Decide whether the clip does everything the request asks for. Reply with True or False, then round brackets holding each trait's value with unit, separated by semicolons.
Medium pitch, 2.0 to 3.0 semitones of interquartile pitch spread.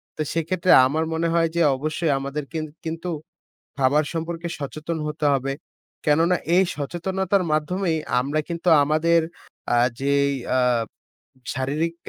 True (160 Hz; 2.7 semitones)